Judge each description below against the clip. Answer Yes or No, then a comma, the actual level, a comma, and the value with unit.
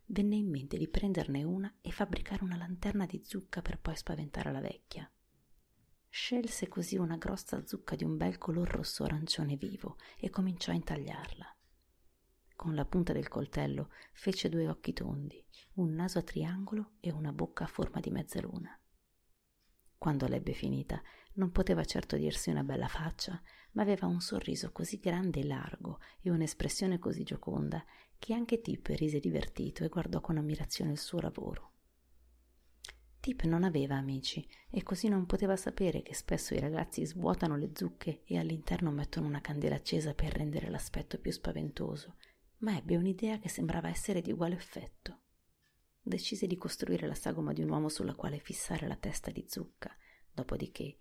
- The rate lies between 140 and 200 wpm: Yes, average, 160 wpm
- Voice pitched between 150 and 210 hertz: Yes, medium, 165 Hz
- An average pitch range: No, wide, 6.1 semitones